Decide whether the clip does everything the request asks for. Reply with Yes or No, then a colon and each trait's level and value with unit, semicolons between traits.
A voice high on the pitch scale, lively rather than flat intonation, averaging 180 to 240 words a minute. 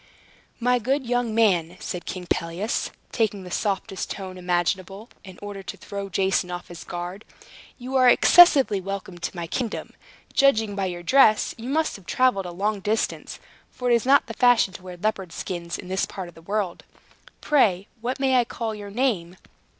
No: high, 200 Hz; average, 4.9 semitones; average, 185 wpm